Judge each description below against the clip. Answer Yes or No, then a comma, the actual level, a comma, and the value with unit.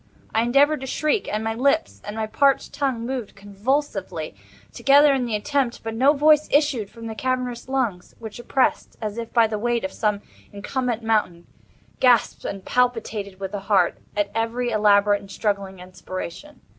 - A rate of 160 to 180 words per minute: Yes, average, 170 wpm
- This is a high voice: Yes, high, 225 Hz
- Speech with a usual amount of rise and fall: Yes, average, 4.3 semitones